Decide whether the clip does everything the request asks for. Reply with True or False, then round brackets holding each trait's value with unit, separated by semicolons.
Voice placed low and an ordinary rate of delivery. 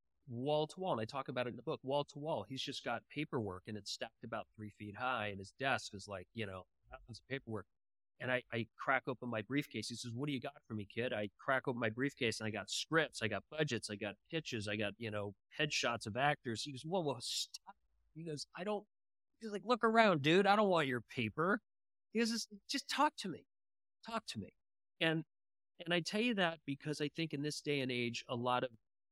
False (130 Hz; 245 wpm)